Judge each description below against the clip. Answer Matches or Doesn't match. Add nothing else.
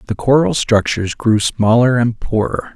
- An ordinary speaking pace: Matches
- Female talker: Doesn't match